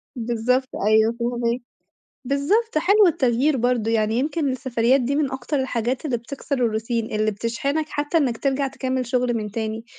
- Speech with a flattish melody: No, average, 3.3 semitones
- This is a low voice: No, very high, 250 Hz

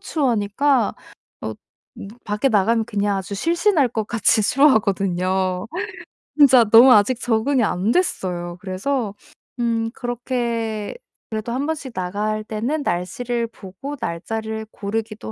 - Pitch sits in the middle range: No, high, 220 Hz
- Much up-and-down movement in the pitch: No, average, 3.7 semitones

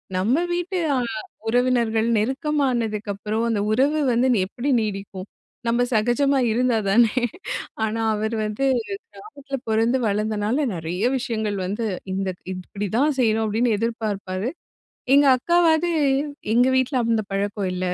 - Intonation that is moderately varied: Yes, average, 3.7 semitones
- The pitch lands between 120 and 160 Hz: No, high, 225 Hz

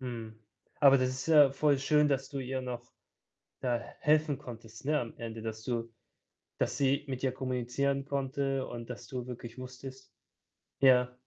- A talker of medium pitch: No, low, 130 Hz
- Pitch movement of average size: No, narrow, 2.2 semitones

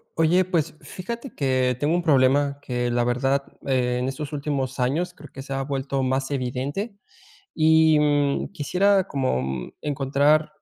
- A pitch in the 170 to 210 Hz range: No, medium, 140 Hz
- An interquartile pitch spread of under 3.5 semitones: Yes, average, 3.1 semitones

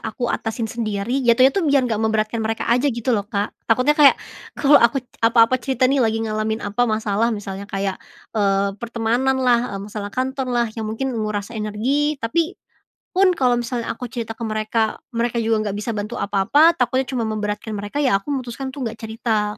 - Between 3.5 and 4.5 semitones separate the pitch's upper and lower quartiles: No, average, 3.1 semitones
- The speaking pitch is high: Yes, high, 230 Hz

